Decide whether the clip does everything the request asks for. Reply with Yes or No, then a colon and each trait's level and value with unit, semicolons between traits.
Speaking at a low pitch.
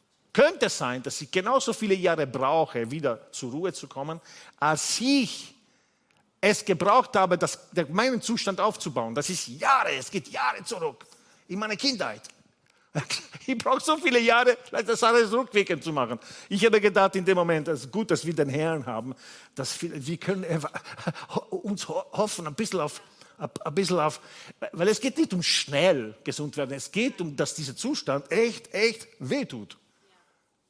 No: medium, 185 Hz